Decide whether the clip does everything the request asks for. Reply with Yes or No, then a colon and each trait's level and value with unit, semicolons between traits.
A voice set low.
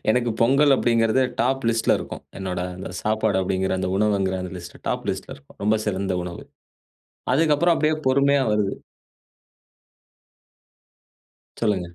Yes: low, 110 Hz